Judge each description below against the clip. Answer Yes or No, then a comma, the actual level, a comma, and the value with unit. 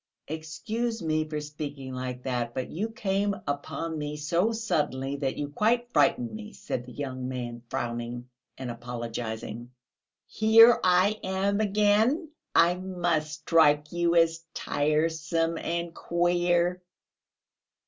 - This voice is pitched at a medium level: Yes, medium, 160 Hz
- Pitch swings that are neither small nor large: No, wide, 6.0 semitones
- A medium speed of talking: No, slow, 125 wpm